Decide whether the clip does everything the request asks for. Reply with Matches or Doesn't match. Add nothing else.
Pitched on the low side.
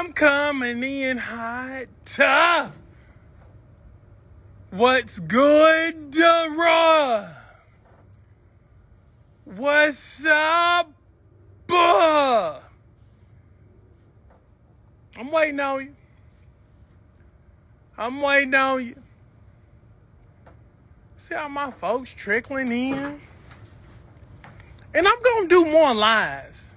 Doesn't match